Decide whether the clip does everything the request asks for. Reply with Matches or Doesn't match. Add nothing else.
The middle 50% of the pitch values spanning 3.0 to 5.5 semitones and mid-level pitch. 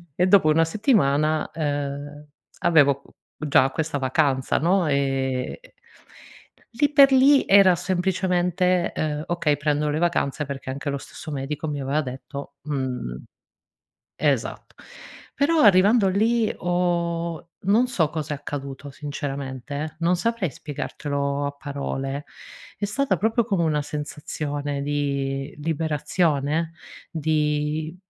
Matches